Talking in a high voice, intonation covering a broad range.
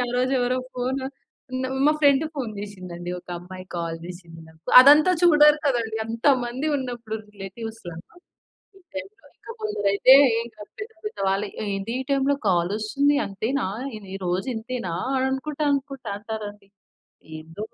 Yes: high, 230 Hz; wide, 5.9 semitones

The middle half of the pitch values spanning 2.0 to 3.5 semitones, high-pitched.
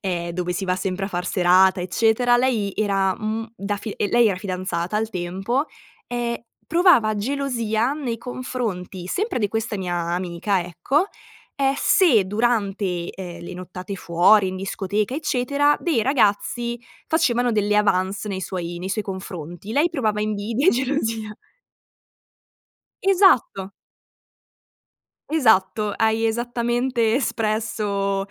No: average, 4.3 semitones; high, 210 Hz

